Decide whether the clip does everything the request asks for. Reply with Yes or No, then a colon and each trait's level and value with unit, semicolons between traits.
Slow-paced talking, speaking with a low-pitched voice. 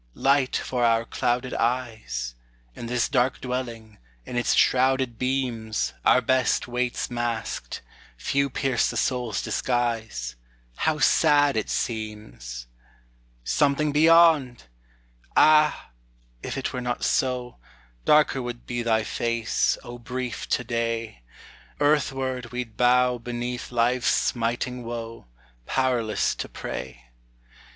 Yes: slow, 115 wpm; low, 120 Hz